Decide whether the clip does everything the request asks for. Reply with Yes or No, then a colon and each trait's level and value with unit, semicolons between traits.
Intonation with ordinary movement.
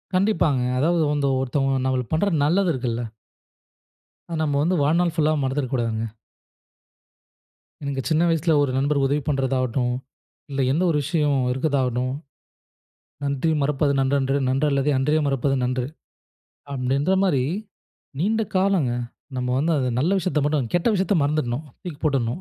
Yes: average, 3.3 semitones